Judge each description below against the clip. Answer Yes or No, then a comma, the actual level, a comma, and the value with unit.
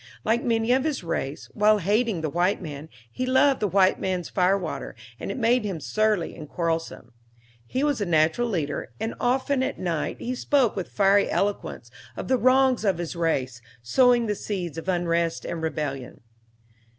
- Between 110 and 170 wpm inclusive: No, average, 180 wpm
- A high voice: Yes, high, 195 Hz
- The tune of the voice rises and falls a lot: Yes, wide, 6.4 semitones